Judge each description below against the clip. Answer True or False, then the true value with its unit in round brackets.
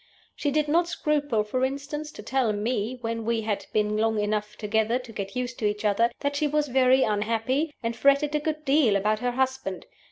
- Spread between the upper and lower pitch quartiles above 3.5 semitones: True (4.9 semitones)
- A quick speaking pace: True (210 wpm)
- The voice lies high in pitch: True (245 Hz)